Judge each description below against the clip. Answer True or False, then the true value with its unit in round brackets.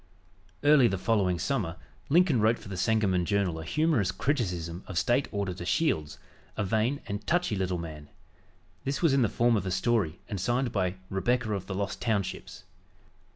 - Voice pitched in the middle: False (100 Hz)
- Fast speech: False (175 wpm)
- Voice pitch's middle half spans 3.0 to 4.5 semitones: False (4.9 semitones)